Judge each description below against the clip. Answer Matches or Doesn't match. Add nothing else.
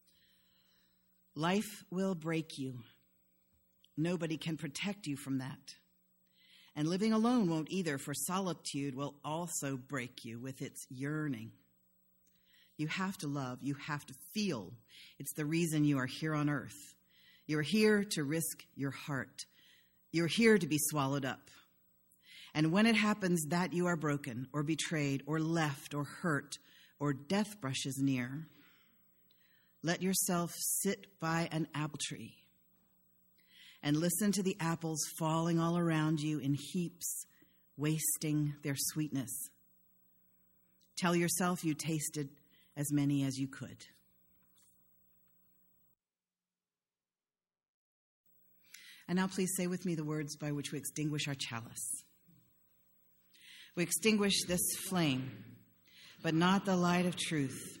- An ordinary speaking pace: Doesn't match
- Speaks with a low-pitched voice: Doesn't match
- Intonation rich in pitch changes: Doesn't match